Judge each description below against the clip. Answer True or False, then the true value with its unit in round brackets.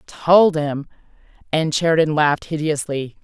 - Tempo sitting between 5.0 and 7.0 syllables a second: False (4.6 syllables/s)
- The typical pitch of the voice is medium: True (155 Hz)